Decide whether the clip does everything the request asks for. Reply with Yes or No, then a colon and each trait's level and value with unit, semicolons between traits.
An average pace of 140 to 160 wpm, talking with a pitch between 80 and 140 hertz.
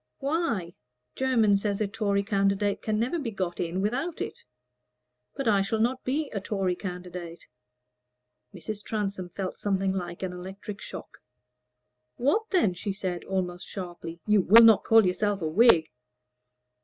No: average, 150 wpm; high, 200 Hz